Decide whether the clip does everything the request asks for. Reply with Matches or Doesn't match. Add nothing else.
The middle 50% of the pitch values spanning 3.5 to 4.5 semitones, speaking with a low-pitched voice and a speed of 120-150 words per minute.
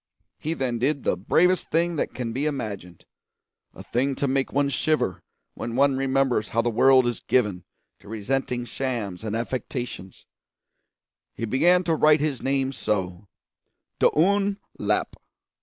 Matches